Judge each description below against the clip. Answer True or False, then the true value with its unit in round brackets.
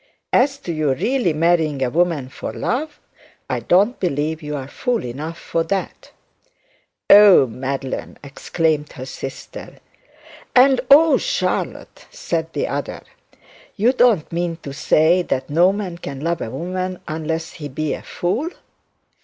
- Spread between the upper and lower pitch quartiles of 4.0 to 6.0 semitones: True (5.2 semitones)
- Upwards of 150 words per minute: False (145 wpm)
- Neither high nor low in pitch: True (165 Hz)